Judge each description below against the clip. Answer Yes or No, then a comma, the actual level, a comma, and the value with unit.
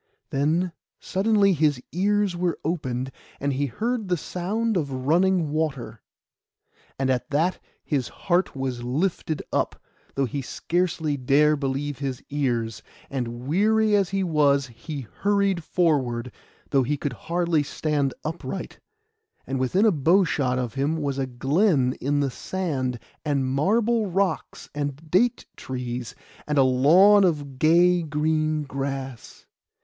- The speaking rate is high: No, slow, 135 wpm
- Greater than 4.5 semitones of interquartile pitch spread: Yes, average, 5.1 semitones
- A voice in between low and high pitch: Yes, medium, 150 Hz